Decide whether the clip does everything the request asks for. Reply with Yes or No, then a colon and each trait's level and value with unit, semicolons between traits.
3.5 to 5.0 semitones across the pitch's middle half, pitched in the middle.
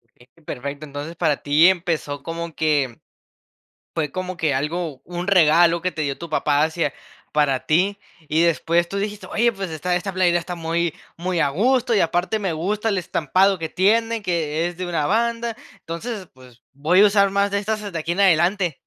Yes: average, 4.1 semitones; medium, 170 Hz